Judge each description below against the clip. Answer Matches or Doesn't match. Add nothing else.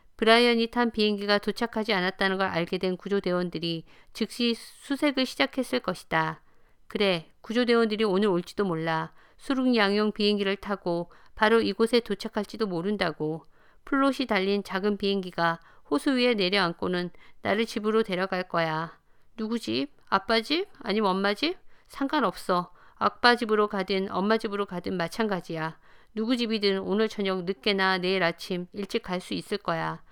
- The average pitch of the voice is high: Matches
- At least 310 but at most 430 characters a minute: Matches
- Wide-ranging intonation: Doesn't match